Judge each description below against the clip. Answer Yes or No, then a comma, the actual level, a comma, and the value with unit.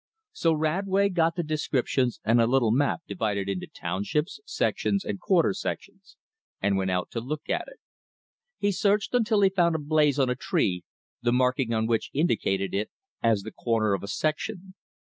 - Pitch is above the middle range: No, medium, 140 Hz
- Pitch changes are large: Yes, wide, 8.3 semitones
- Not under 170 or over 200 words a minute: Yes, average, 180 wpm